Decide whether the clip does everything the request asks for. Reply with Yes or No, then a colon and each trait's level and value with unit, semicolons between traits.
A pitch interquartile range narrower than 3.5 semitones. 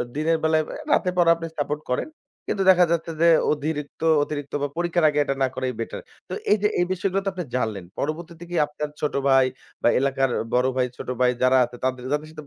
No: average, 4.2 semitones